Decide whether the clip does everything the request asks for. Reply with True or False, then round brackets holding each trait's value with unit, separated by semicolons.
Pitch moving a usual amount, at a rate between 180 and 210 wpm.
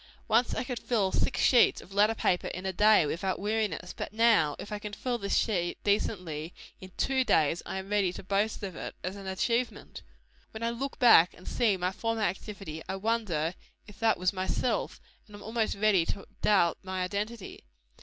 True (3.3 semitones; 195 wpm)